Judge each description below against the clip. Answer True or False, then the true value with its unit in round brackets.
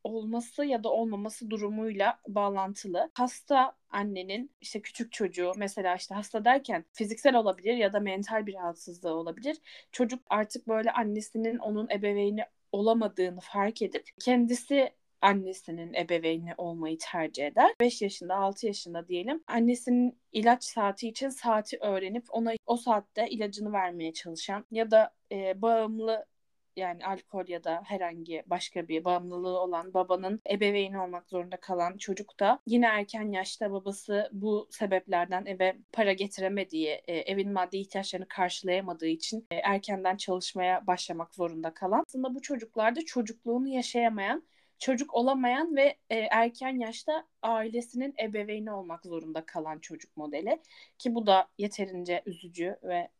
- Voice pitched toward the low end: False (205 Hz)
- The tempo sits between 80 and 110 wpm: False (130 wpm)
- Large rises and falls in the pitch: False (4.2 semitones)